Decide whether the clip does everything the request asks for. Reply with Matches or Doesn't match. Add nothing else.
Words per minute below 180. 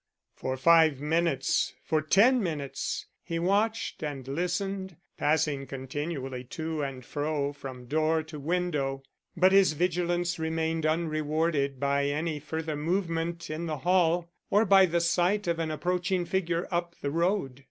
Matches